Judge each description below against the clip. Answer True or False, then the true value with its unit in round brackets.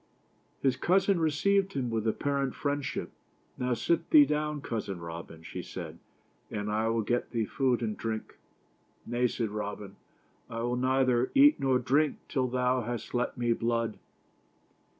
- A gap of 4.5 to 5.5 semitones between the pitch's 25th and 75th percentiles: False (3.7 semitones)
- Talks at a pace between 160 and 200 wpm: True (170 wpm)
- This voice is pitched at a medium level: False (125 Hz)